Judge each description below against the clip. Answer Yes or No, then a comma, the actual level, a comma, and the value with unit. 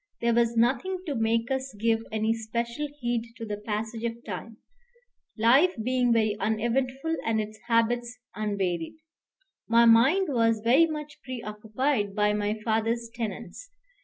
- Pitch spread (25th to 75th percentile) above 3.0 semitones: No, narrow, 2.4 semitones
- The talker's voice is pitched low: No, high, 230 Hz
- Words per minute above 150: No, average, 140 wpm